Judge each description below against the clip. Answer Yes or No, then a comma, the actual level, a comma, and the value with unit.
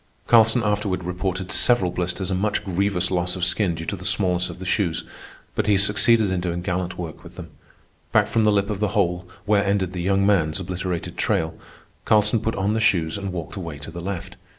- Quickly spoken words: Yes, fast, 215 wpm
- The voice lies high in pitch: No, very low, 95 Hz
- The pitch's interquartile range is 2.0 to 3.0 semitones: Yes, narrow, 2.6 semitones